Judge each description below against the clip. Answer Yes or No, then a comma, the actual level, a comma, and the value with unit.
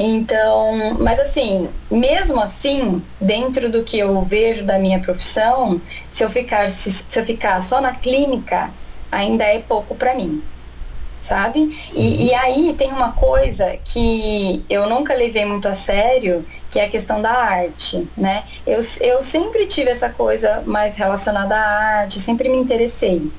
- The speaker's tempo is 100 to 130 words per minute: No, average, 160 wpm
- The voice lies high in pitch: Yes, high, 220 Hz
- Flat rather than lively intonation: No, average, 4.3 semitones